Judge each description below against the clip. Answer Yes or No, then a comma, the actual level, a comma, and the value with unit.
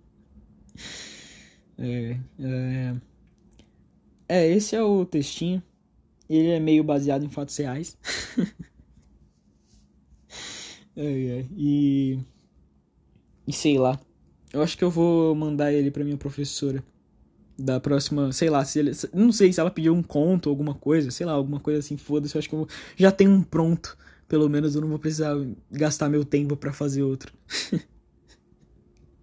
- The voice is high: No, medium, 145 Hz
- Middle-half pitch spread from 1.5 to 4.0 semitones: Yes, average, 3.1 semitones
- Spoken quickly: No, average, 150 wpm